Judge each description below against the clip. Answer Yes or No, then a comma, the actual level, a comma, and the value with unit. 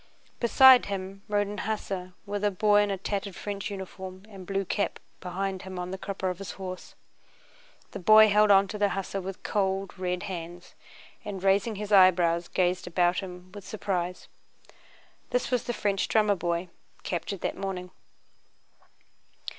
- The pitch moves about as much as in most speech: No, narrow, 2.0 semitones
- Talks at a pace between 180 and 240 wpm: No, average, 160 wpm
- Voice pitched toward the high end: Yes, high, 195 Hz